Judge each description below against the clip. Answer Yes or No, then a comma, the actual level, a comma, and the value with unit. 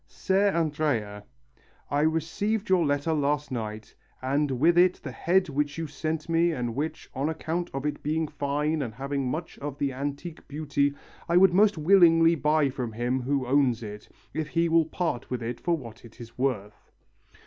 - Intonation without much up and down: No, average, 4.0 semitones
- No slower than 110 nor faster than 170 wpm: No, average, 180 wpm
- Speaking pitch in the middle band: Yes, medium, 145 Hz